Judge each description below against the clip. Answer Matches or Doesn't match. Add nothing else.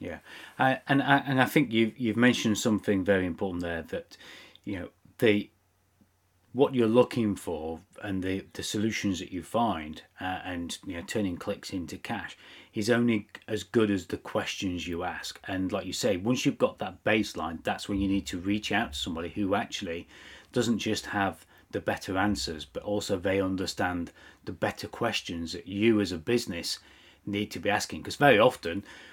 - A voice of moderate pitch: Doesn't match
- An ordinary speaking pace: Matches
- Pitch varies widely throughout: Doesn't match